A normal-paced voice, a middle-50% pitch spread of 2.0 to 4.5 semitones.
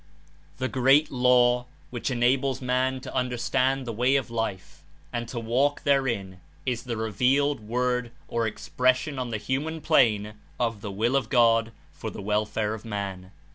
Yes: average, 160 wpm; average, 2.9 semitones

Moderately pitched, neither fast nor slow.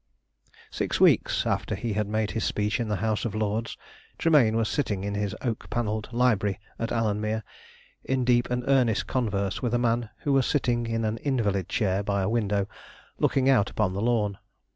No: low, 110 Hz; average, 185 wpm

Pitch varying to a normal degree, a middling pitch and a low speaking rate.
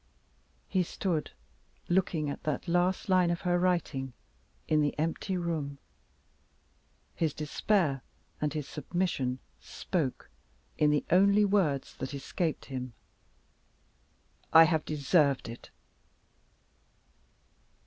Yes: average, 4.0 semitones; medium, 160 Hz; slow, 105 wpm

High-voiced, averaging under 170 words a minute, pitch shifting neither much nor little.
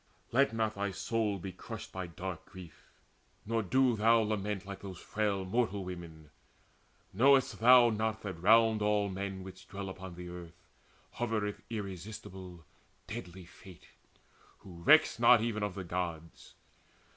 No: low, 100 Hz; average, 145 wpm; average, 3.4 semitones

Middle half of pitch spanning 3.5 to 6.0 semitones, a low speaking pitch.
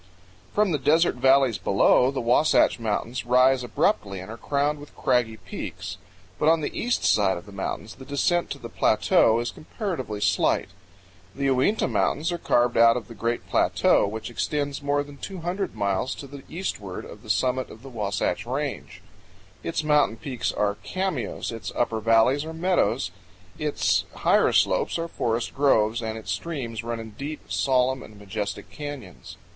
Yes: average, 4.6 semitones; low, 125 Hz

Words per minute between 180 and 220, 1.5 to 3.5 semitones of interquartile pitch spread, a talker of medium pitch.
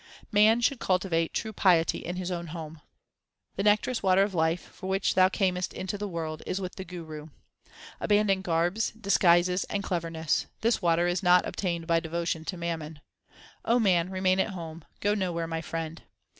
Yes: average, 185 wpm; average, 2.7 semitones; medium, 180 Hz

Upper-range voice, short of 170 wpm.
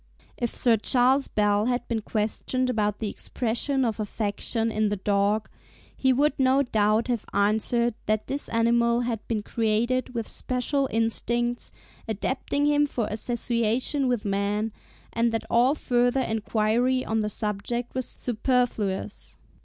Yes: high, 230 Hz; average, 140 wpm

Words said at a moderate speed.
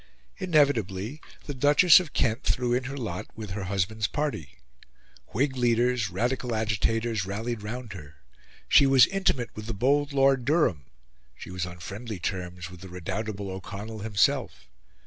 Yes: average, 150 wpm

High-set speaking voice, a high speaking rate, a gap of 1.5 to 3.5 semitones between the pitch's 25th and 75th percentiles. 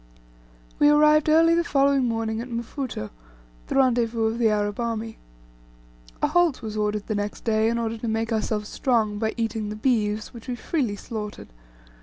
No: high, 225 Hz; average, 175 wpm; average, 3.0 semitones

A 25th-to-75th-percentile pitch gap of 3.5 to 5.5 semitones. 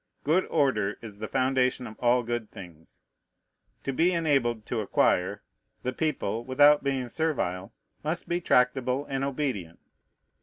Yes: average, 4.7 semitones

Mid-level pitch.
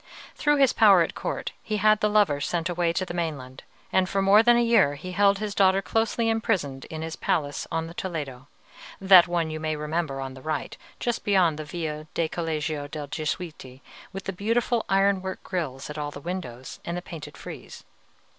Yes: medium, 170 Hz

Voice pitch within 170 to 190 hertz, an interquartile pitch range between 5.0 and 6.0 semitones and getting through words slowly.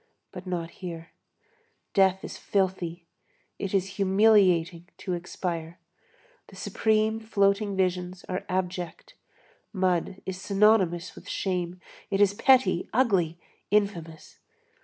No: medium, 185 Hz; narrow, 2.4 semitones; slow, 110 wpm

